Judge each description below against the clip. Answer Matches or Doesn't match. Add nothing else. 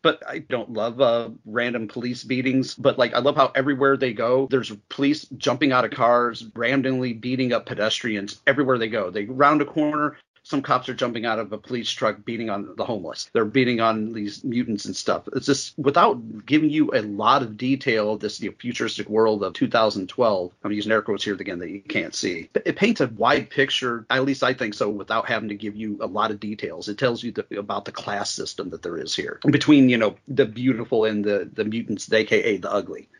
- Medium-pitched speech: Doesn't match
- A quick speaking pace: Matches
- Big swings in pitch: Doesn't match